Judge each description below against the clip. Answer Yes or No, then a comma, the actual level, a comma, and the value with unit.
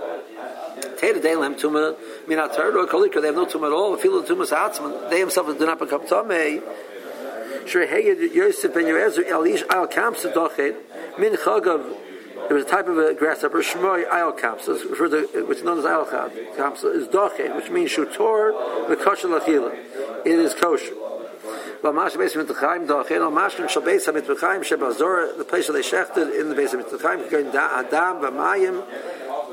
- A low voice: No, very high, 385 Hz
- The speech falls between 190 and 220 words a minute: Yes, average, 200 wpm